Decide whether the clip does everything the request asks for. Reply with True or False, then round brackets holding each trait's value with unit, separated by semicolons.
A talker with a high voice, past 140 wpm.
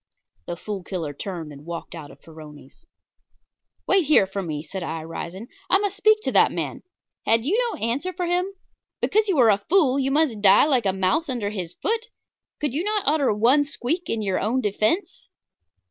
True (230 Hz; 195 wpm)